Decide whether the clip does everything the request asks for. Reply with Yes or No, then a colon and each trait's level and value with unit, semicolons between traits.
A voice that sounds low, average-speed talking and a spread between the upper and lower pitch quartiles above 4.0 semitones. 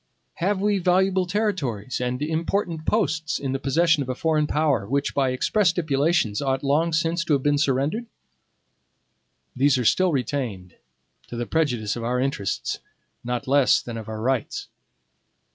No: medium, 145 Hz; average, 160 wpm; average, 4.9 semitones